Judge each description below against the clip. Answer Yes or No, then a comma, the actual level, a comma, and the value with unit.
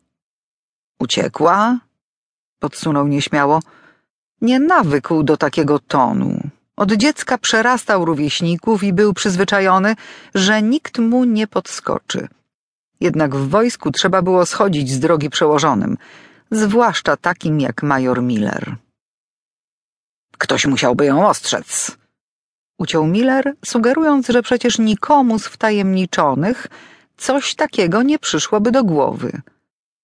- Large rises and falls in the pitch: Yes, wide, 7.2 semitones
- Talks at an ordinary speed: No, slow, 105 wpm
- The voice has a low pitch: No, high, 205 Hz